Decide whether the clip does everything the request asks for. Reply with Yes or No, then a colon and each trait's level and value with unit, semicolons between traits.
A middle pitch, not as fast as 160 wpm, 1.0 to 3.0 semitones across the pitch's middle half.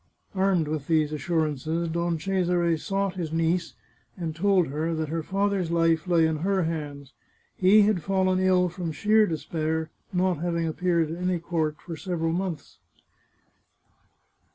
Yes: medium, 170 Hz; average, 150 wpm; narrow, 2.6 semitones